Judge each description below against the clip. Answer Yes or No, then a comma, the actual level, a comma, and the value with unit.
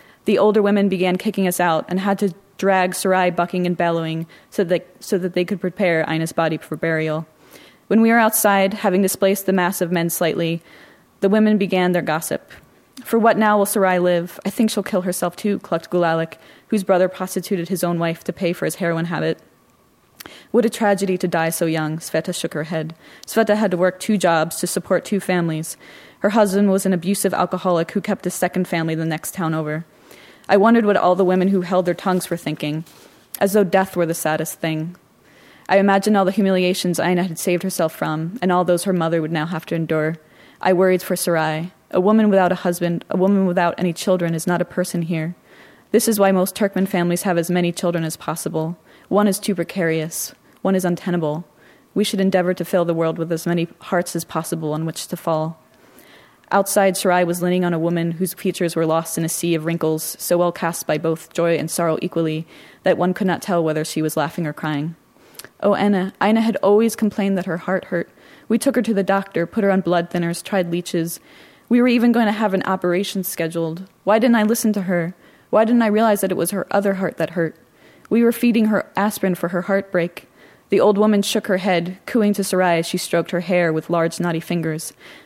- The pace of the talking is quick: Yes, fast, 220 wpm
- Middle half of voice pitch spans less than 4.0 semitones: Yes, average, 2.9 semitones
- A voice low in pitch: No, medium, 180 Hz